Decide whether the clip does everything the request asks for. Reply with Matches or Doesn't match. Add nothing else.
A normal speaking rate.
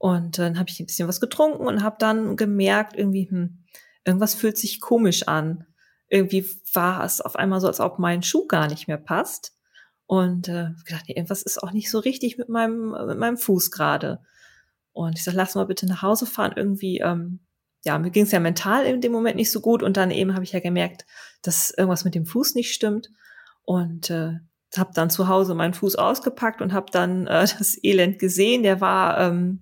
Doesn't match